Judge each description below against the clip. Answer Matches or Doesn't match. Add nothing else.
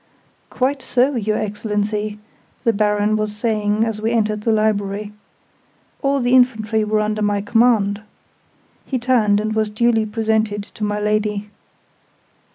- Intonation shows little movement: Matches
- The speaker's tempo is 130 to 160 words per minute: Matches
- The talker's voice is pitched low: Doesn't match